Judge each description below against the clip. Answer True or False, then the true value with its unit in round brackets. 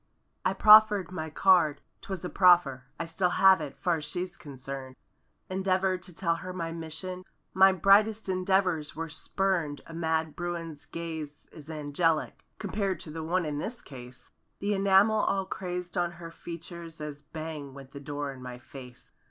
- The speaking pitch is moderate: True (170 Hz)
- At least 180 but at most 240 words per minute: False (160 wpm)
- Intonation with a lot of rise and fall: False (3.8 semitones)